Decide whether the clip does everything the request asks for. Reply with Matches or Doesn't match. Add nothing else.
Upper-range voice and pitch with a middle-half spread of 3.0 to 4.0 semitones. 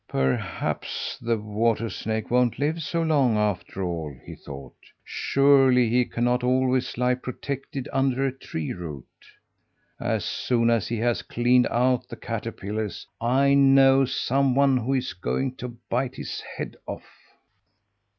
Doesn't match